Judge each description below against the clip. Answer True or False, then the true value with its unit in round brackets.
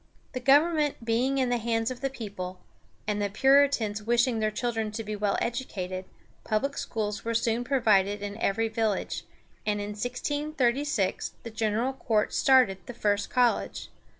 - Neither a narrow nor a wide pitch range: True (3.6 semitones)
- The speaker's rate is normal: True (155 wpm)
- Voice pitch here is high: True (225 Hz)